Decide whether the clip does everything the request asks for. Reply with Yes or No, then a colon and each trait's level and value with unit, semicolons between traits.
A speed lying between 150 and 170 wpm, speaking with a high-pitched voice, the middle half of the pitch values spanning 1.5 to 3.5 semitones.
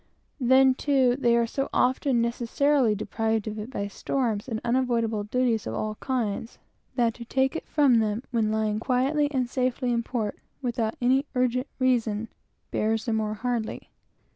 Yes: average, 160 wpm; high, 240 Hz; average, 2.7 semitones